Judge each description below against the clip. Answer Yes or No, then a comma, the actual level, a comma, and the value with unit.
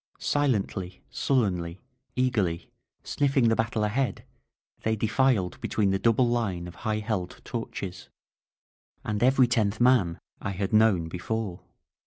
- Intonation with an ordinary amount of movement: Yes, average, 4.5 semitones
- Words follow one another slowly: Yes, slow, 130 wpm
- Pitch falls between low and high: No, low, 110 Hz